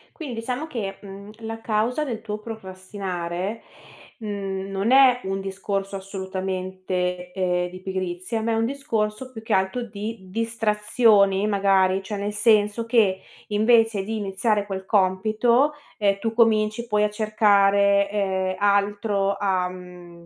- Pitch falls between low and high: No, high, 205 Hz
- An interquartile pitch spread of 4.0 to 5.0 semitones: No, average, 2.7 semitones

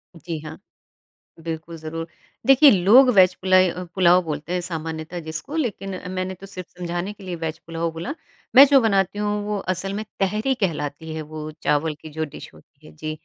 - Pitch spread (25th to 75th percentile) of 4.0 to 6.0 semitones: No, average, 3.6 semitones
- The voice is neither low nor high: Yes, medium, 175 Hz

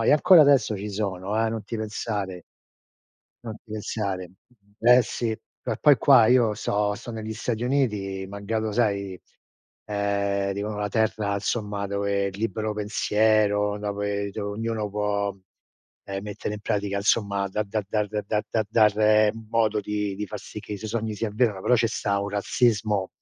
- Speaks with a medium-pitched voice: No, low, 105 Hz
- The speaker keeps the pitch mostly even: Yes, narrow, 1.6 semitones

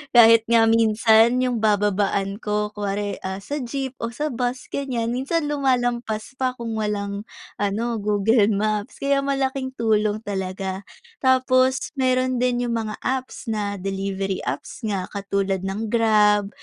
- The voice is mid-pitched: No, high, 220 Hz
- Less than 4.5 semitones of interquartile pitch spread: Yes, average, 3.7 semitones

